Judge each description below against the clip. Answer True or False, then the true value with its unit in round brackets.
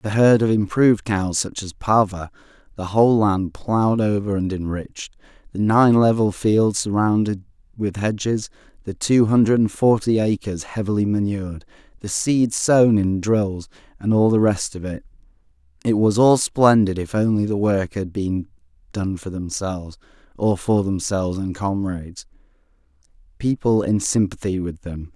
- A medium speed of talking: True (150 wpm)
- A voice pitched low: True (100 Hz)